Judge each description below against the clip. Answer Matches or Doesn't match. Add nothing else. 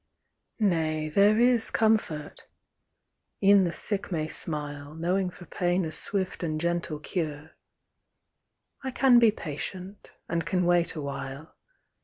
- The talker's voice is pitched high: Doesn't match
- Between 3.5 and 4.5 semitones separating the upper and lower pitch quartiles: Matches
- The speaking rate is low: Matches